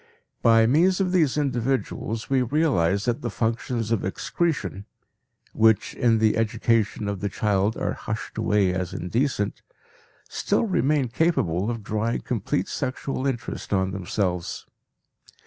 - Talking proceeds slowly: Yes, slow, 130 wpm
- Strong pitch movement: No, average, 4.4 semitones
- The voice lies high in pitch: No, low, 115 Hz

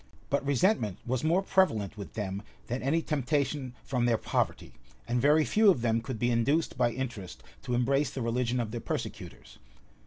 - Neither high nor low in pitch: No, low, 125 Hz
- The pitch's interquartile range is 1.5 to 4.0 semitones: Yes, average, 3.7 semitones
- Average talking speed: Yes, average, 180 wpm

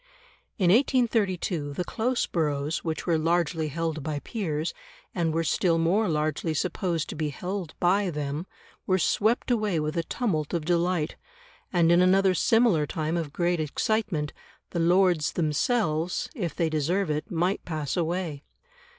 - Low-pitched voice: No, medium, 170 Hz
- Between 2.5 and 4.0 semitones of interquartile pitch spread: Yes, average, 3.3 semitones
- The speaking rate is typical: Yes, average, 150 wpm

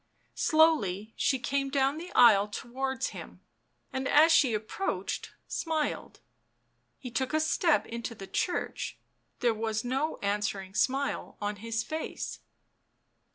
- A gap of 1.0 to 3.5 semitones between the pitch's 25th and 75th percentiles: No, wide, 5.4 semitones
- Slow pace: Yes, slow, 125 wpm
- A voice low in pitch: No, very high, 255 Hz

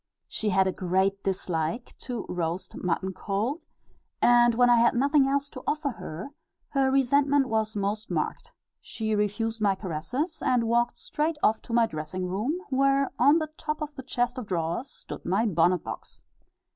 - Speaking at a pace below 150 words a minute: No, average, 170 wpm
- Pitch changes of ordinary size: No, wide, 6.1 semitones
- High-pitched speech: Yes, high, 225 Hz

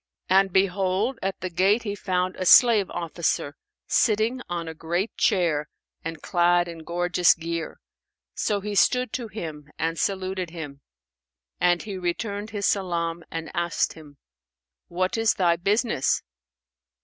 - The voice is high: No, medium, 180 Hz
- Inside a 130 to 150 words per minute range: Yes, average, 140 wpm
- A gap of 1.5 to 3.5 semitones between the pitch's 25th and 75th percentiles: Yes, average, 3.2 semitones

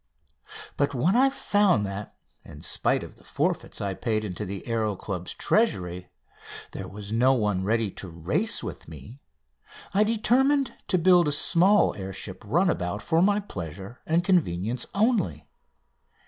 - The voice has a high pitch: No, low, 120 Hz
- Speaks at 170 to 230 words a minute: No, average, 150 wpm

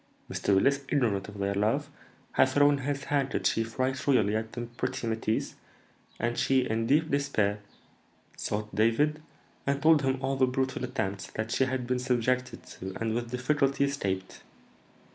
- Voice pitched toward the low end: Yes, low, 125 Hz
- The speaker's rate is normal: Yes, average, 160 wpm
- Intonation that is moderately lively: Yes, average, 3.7 semitones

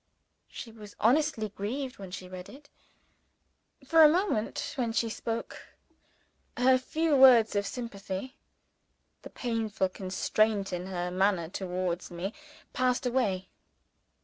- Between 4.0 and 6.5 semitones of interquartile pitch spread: Yes, average, 5.1 semitones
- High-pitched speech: Yes, high, 220 Hz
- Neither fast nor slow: No, slow, 120 wpm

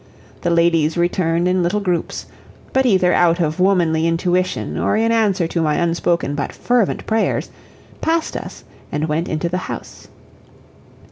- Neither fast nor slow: Yes, average, 150 wpm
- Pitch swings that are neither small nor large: No, narrow, 2.3 semitones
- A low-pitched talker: No, medium, 175 Hz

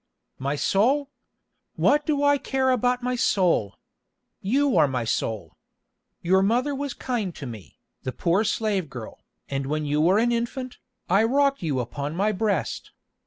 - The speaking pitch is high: Yes, high, 200 Hz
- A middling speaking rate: Yes, average, 160 wpm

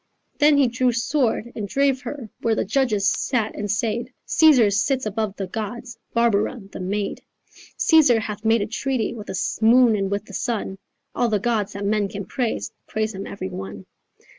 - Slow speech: No, average, 185 wpm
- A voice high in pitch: Yes, high, 220 Hz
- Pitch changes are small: No, average, 3.2 semitones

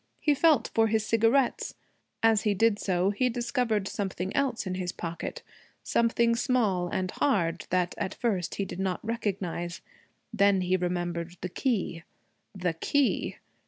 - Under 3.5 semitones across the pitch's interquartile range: No, average, 4.4 semitones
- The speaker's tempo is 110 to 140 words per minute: No, average, 150 wpm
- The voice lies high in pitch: Yes, high, 200 Hz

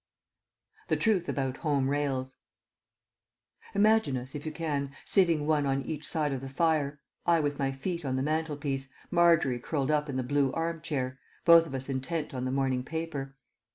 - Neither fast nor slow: Yes, average, 180 wpm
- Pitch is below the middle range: No, medium, 145 Hz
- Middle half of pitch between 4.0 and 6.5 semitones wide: No, average, 3.2 semitones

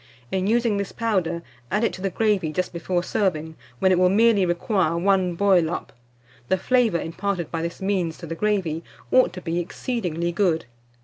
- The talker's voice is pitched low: No, medium, 185 Hz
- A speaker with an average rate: Yes, average, 185 wpm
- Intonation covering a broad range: No, average, 3.1 semitones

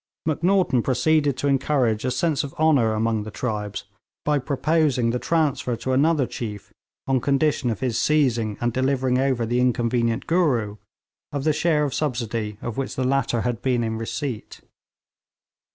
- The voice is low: Yes, low, 130 Hz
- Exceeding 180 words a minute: No, average, 160 wpm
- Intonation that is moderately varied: Yes, average, 3.9 semitones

